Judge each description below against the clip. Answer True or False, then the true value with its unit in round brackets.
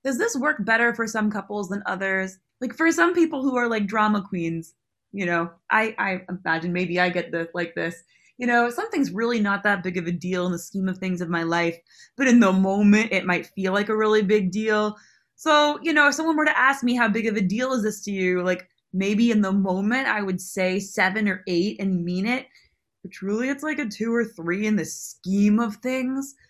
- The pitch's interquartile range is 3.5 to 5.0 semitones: True (4.3 semitones)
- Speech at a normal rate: False (235 wpm)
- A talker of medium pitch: False (205 Hz)